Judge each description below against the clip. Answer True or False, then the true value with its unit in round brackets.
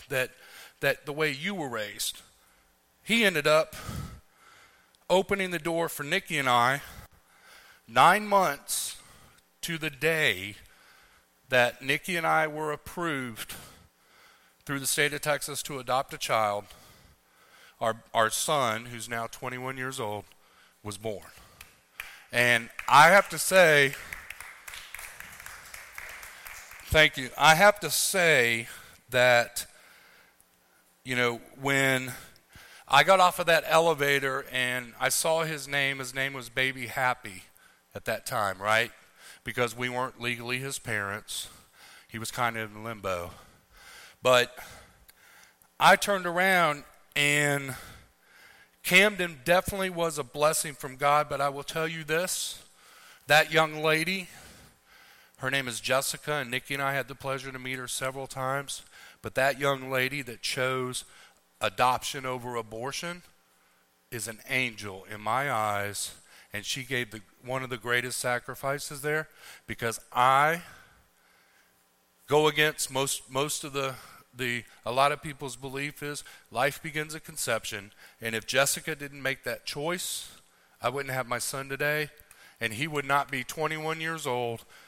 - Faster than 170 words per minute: False (140 wpm)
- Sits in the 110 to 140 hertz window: True (135 Hz)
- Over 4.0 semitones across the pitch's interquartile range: True (4.4 semitones)